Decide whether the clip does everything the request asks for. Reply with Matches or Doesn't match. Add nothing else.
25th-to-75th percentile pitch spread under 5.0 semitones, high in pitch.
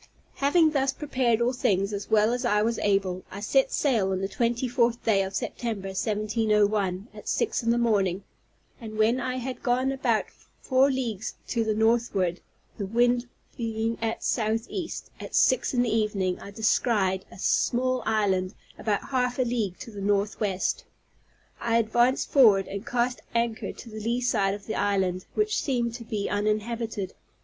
Matches